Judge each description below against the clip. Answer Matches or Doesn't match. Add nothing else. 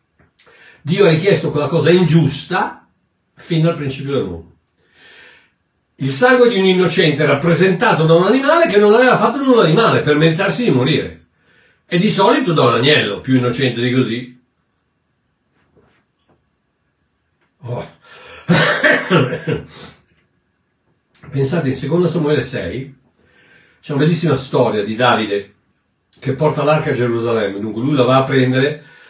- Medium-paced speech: Matches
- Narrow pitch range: Doesn't match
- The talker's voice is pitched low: Doesn't match